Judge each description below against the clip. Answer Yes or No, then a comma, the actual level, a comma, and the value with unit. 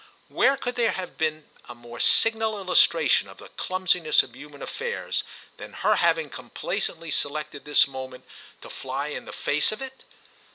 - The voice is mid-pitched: Yes, medium, 155 Hz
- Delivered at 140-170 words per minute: Yes, average, 165 wpm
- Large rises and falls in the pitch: Yes, wide, 7.7 semitones